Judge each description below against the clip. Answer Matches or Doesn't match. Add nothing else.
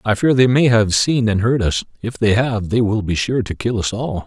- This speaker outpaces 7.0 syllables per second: Doesn't match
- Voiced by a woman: Doesn't match